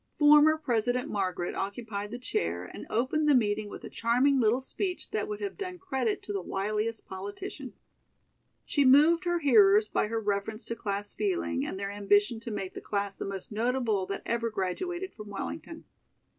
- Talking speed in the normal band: Yes, average, 180 wpm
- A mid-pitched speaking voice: No, high, 225 Hz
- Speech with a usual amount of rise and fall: No, wide, 5.7 semitones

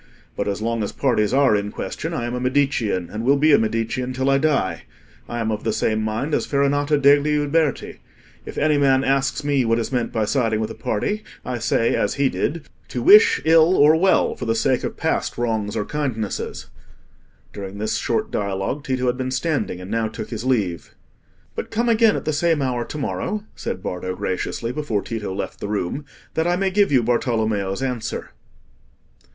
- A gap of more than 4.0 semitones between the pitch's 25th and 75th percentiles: Yes, average, 4.8 semitones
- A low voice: Yes, low, 125 Hz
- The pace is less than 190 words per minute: No, average, 200 wpm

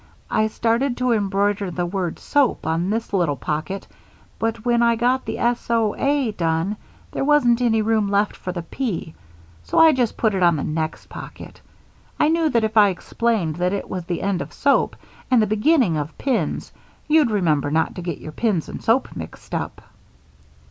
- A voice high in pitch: Yes, high, 210 Hz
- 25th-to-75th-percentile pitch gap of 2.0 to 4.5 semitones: No, average, 5.3 semitones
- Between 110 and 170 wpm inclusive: No, average, 190 wpm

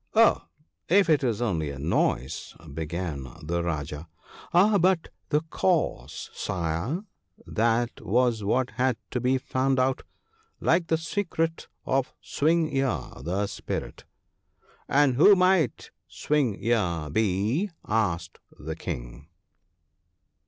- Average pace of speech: No, slow, 130 wpm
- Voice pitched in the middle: No, low, 120 Hz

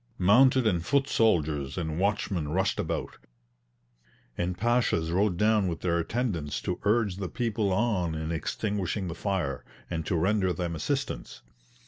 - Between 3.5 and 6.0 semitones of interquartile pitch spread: Yes, average, 4.6 semitones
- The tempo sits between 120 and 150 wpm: Yes, average, 145 wpm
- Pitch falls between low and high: No, very low, 95 Hz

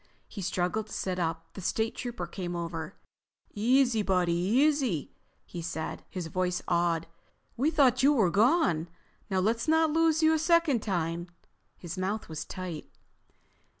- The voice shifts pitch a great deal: Yes, wide, 6.8 semitones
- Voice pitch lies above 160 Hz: Yes, high, 190 Hz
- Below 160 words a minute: Yes, average, 150 wpm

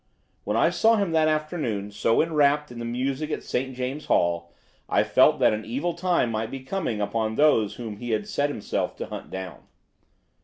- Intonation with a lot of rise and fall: Yes, wide, 5.8 semitones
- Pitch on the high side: No, low, 130 Hz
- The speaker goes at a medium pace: Yes, average, 195 wpm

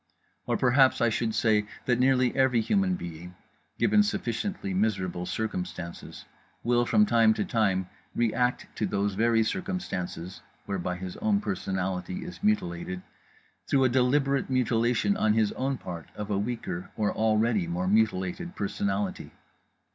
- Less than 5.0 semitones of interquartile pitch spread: No, wide, 5.4 semitones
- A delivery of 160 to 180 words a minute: No, average, 140 wpm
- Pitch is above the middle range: No, low, 110 Hz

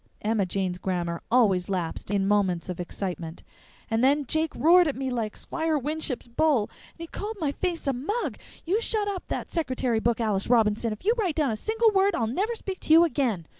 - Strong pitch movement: Yes, wide, 8.2 semitones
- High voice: Yes, very high, 255 Hz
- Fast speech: Yes, fast, 210 wpm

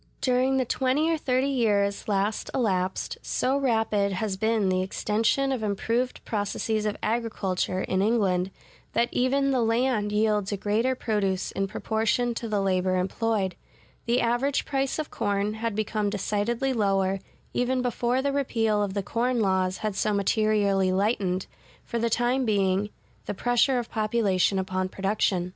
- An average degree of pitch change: Yes, average, 3.6 semitones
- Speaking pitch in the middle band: No, high, 215 Hz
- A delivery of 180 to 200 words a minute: No, average, 155 wpm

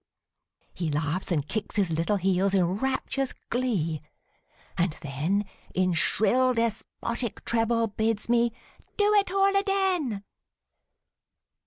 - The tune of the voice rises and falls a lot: Yes, wide, 5.9 semitones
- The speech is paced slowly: Yes, slow, 115 wpm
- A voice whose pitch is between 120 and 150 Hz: No, high, 215 Hz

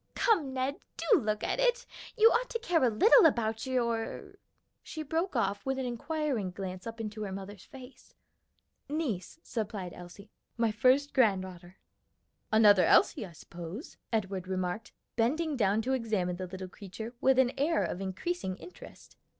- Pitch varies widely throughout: Yes, wide, 6.4 semitones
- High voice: Yes, high, 225 Hz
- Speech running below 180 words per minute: Yes, average, 160 wpm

